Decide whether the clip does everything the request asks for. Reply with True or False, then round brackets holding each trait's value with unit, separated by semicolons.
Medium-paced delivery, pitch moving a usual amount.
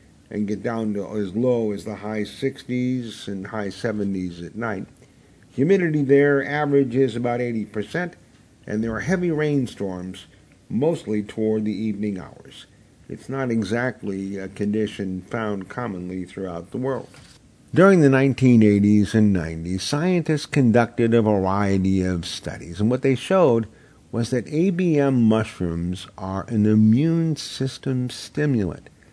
False (130 wpm; 4.9 semitones)